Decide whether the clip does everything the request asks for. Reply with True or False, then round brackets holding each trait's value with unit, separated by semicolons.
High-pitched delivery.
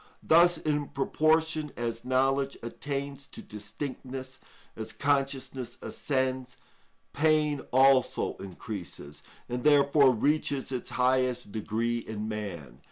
False (130 Hz)